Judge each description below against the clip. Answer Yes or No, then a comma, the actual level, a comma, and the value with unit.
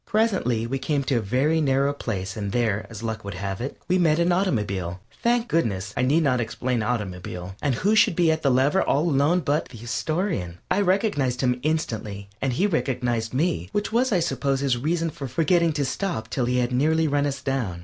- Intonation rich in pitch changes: Yes, wide, 6.1 semitones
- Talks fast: Yes, fast, 210 wpm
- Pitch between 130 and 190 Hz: Yes, low, 135 Hz